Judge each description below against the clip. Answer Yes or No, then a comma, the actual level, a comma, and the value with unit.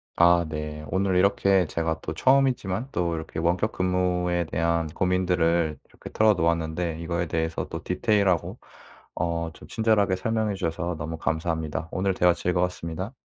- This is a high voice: No, very low, 90 Hz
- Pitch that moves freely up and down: No, narrow, 2.3 semitones